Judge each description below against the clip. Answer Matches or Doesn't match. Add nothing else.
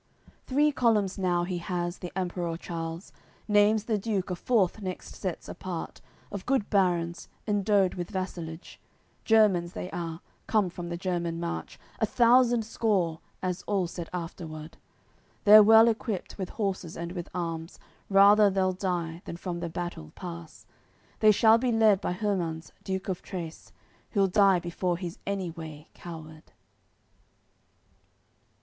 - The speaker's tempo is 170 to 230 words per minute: Doesn't match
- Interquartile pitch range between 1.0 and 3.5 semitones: Matches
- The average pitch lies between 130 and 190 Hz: Matches